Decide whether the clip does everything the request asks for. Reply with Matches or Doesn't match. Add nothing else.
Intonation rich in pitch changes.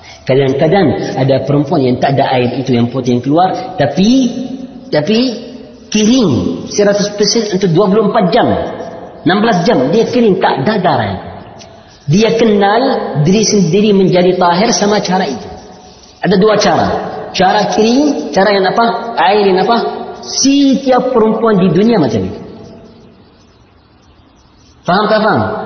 Matches